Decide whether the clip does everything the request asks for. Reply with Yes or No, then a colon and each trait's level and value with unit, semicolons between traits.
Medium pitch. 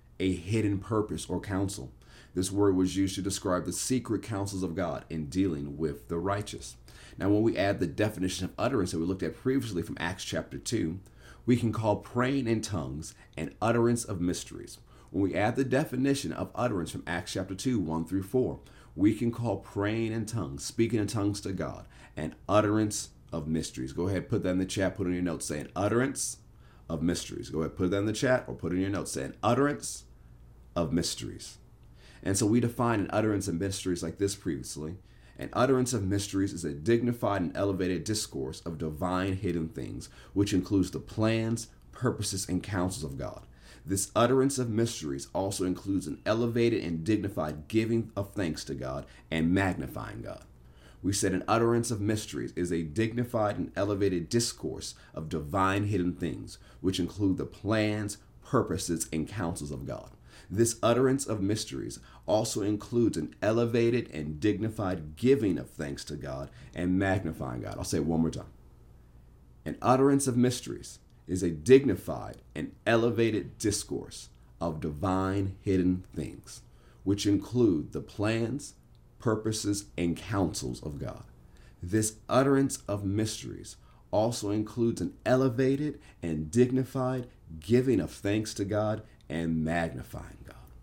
No: low, 100 Hz